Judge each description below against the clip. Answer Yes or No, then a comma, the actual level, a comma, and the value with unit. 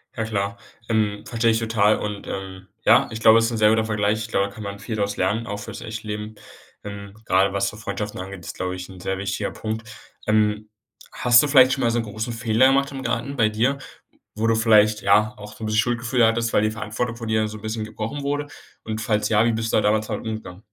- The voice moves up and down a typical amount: No, narrow, 1.7 semitones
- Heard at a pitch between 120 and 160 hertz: No, low, 110 Hz